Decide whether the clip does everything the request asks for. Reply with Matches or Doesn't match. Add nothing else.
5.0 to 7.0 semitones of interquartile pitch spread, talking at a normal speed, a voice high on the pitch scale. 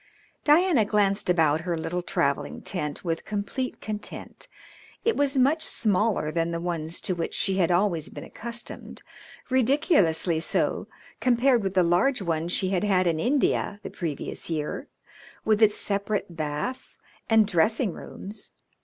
Matches